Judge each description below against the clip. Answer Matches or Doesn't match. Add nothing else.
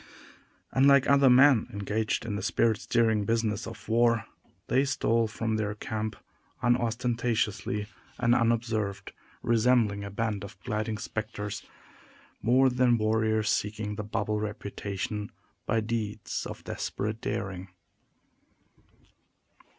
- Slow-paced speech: Matches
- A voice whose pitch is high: Doesn't match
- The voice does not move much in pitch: Matches